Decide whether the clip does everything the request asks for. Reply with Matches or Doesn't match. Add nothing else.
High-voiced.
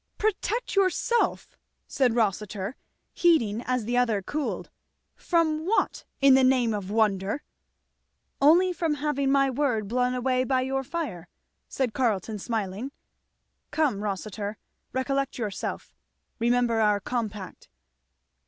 Matches